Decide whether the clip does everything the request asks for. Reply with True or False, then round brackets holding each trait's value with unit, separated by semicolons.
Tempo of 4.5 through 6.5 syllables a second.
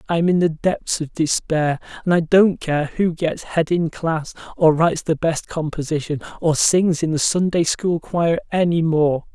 False (4.3 syllables/s)